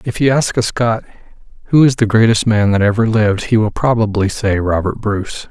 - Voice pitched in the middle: No, low, 110 Hz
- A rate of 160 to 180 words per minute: No, fast, 205 wpm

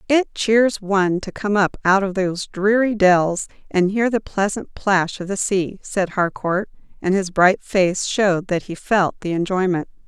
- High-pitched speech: Yes, high, 195 Hz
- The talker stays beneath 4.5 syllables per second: Yes, 4.3 syllables/s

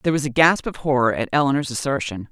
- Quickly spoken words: Yes, fast, 235 wpm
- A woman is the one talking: Yes, female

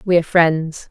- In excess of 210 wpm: No, average, 200 wpm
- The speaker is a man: No, female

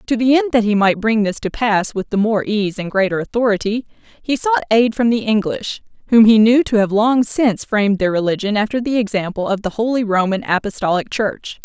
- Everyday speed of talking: No, fast, 215 wpm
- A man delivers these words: No, female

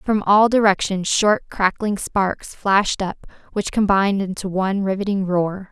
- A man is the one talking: No, female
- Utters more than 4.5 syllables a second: No, 4.4 syllables/s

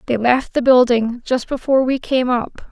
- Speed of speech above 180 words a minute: Yes, average, 200 wpm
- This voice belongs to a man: No, female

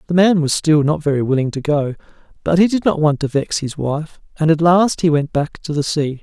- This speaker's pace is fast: Yes, fast, 260 wpm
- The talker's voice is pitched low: No, medium, 155 Hz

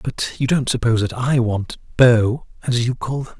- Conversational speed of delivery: No, fast, 210 wpm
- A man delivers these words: Yes, male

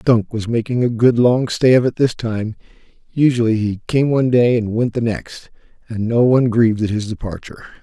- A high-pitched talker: No, low, 115 Hz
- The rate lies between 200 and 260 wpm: Yes, fast, 205 wpm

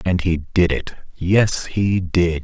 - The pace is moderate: Yes, average, 175 wpm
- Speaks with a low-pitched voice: Yes, very low, 90 Hz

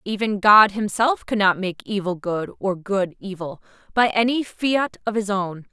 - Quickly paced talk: No, average, 170 wpm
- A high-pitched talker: Yes, high, 205 Hz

